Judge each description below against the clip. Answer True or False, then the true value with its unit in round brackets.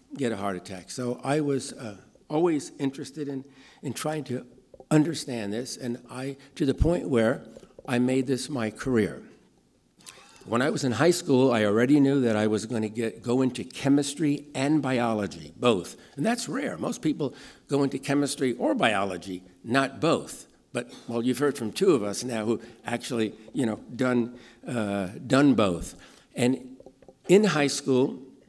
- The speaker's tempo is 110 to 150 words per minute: False (170 wpm)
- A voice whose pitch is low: True (130 Hz)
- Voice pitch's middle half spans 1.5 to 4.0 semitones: True (3.5 semitones)